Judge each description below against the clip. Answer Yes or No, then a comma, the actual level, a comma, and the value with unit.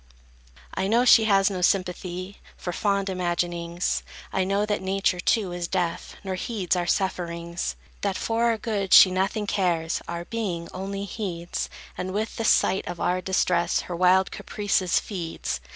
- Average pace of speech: Yes, average, 160 wpm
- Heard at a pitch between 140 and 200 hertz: Yes, medium, 185 Hz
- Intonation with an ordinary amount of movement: No, narrow, 2.3 semitones